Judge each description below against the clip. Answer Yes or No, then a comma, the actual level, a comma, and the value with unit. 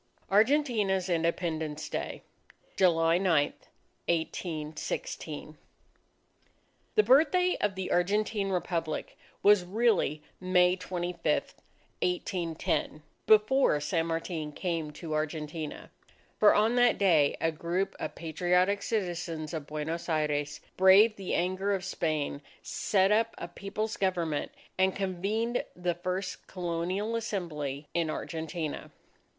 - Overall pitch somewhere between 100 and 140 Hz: No, medium, 180 Hz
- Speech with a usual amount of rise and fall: Yes, average, 3.7 semitones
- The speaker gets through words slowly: Yes, slow, 110 wpm